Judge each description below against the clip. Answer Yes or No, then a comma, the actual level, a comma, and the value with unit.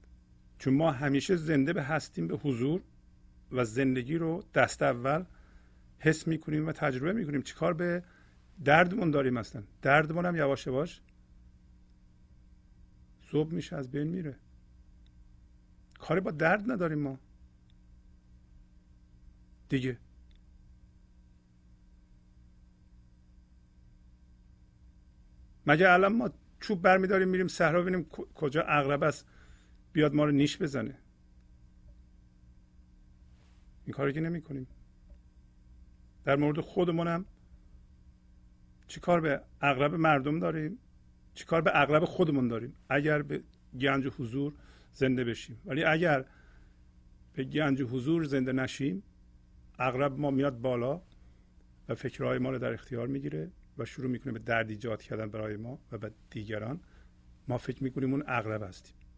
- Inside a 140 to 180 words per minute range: No, average, 120 wpm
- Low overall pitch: Yes, low, 110 Hz